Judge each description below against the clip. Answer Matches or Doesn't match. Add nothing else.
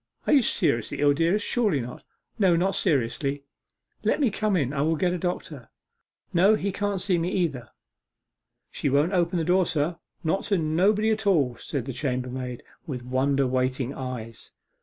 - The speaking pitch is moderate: Matches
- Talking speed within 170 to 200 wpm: Matches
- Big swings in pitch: Matches